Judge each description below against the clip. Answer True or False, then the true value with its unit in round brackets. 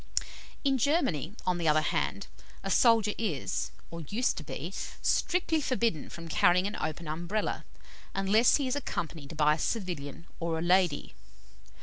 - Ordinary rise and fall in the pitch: False (6.3 semitones)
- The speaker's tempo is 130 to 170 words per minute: True (150 wpm)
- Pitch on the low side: False (180 Hz)